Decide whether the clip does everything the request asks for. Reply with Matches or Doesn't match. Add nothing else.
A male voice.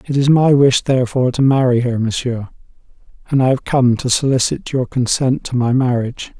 Matches